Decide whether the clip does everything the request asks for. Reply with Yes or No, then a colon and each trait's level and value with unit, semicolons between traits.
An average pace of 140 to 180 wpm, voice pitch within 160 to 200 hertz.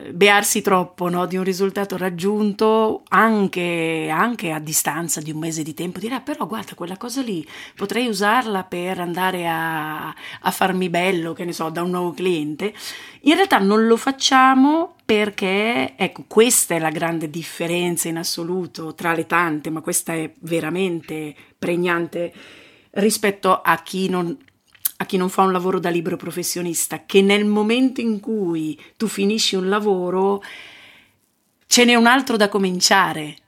Yes: average, 160 wpm; medium, 185 Hz